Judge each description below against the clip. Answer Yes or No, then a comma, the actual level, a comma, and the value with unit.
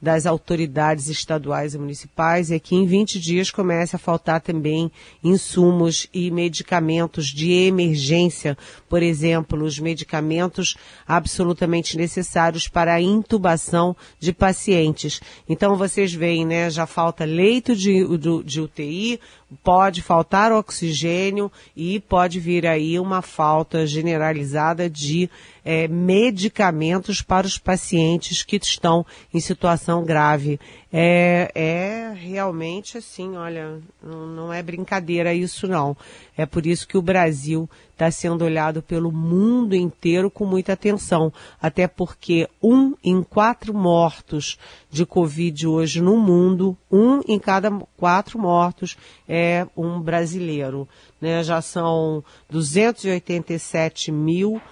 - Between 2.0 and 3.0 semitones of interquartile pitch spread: Yes, narrow, 2.5 semitones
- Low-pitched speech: No, medium, 170 Hz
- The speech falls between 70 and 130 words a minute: Yes, slow, 120 wpm